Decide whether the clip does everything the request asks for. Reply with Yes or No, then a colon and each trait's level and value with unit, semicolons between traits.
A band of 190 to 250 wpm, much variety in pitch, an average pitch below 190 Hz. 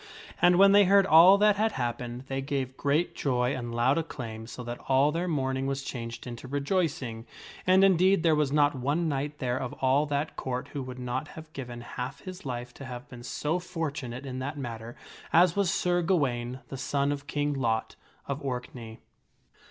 No: average, 195 wpm; average, 4.5 semitones; low, 135 Hz